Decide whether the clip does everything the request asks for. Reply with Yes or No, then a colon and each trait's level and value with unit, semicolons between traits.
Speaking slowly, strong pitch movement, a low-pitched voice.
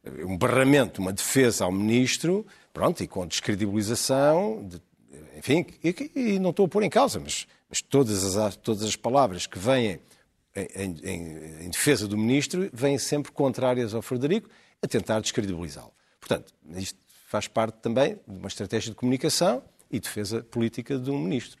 No: average, 165 wpm; wide, 5.8 semitones; low, 120 Hz